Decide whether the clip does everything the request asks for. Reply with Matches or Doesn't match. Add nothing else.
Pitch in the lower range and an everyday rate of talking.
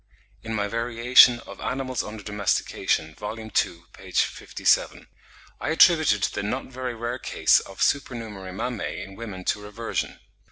Matches